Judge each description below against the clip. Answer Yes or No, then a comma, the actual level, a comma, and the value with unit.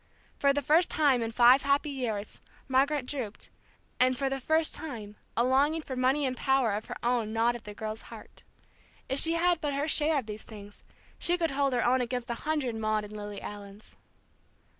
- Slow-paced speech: No, fast, 205 wpm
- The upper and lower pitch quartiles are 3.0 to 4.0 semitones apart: No, average, 4.4 semitones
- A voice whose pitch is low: No, very high, 255 Hz